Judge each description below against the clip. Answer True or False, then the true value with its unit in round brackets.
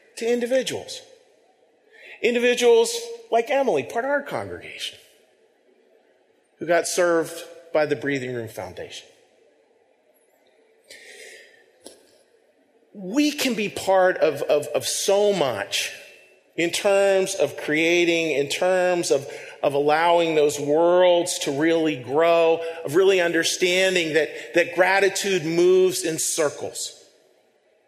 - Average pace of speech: False (105 wpm)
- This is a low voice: False (185 Hz)